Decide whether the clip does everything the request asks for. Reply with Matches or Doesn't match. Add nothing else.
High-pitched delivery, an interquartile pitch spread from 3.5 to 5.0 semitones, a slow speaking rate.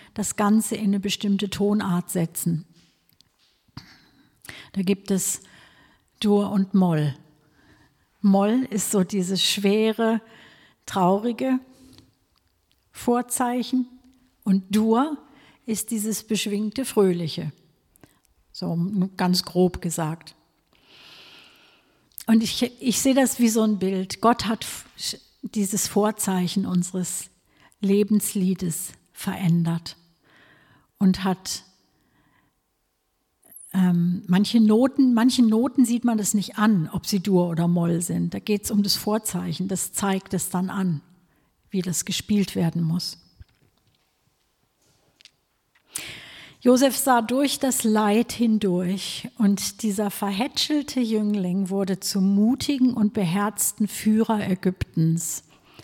Matches